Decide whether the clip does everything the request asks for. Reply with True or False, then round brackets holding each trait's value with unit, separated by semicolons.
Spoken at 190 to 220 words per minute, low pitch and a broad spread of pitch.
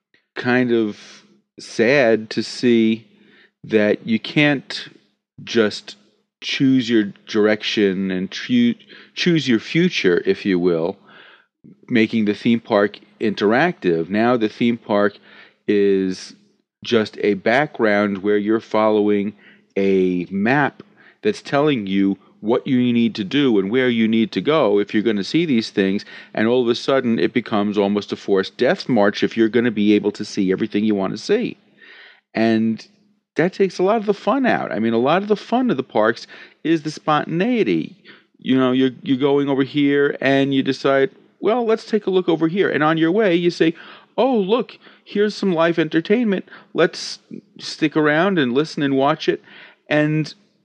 False (170 wpm; 125 Hz; 7.4 semitones)